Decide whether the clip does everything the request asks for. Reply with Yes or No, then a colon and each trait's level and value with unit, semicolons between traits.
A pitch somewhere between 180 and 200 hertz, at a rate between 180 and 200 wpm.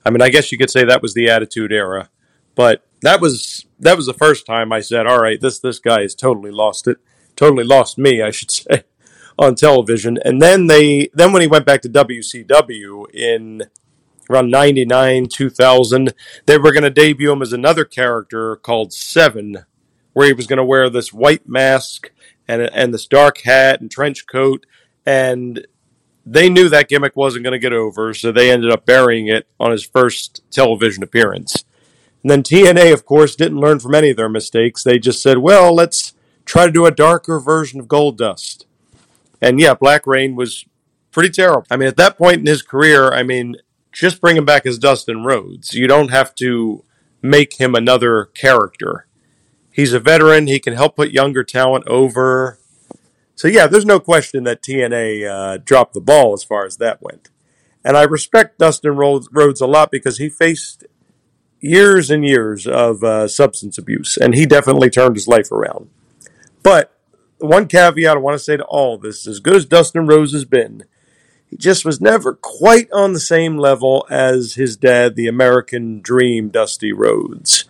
No: low, 135 Hz; average, 190 wpm